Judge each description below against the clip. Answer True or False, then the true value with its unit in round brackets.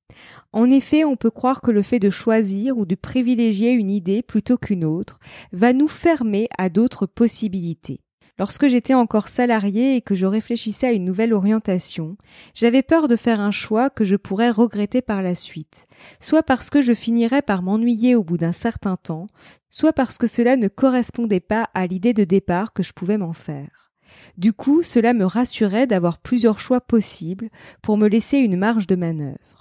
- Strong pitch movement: False (3.9 semitones)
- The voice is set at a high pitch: True (220 Hz)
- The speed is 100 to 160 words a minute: False (190 wpm)